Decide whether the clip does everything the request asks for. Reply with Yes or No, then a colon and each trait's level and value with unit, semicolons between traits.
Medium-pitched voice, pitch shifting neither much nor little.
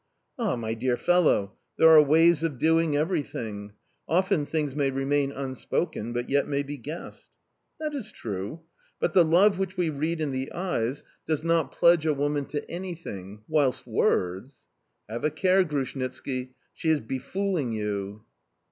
Yes: medium, 145 Hz; average, 4.7 semitones